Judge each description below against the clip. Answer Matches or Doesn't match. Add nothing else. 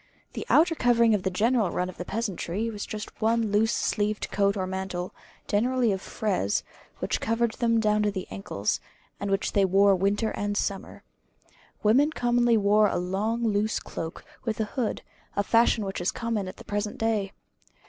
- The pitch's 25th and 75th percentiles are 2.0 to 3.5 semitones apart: Matches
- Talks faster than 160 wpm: Matches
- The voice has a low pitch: Doesn't match